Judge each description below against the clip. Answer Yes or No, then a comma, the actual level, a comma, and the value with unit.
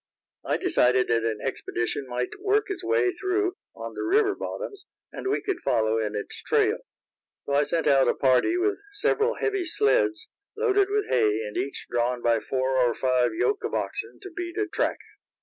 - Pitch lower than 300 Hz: No, very high, 340 Hz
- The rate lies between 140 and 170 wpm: No, average, 185 wpm